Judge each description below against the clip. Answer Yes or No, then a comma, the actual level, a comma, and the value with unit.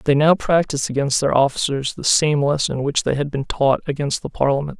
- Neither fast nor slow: No, fast, 215 wpm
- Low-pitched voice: No, medium, 145 Hz